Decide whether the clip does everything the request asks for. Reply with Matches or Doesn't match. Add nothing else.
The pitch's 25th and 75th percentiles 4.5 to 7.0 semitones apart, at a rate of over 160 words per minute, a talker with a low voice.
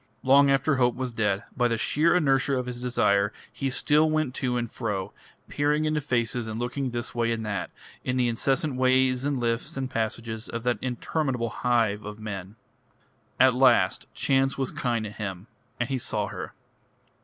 Doesn't match